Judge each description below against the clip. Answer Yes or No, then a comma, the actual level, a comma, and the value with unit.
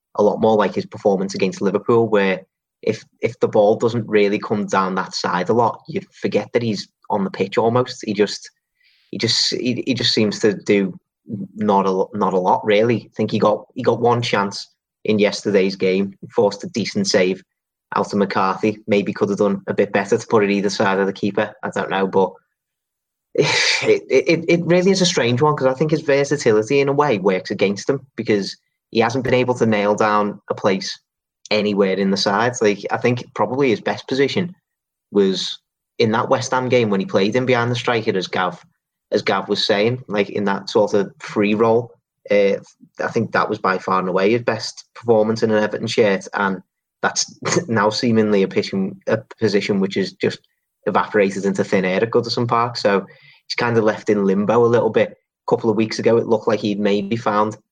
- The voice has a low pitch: Yes, low, 110 Hz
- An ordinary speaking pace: No, fast, 215 wpm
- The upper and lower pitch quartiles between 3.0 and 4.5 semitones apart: Yes, average, 3.8 semitones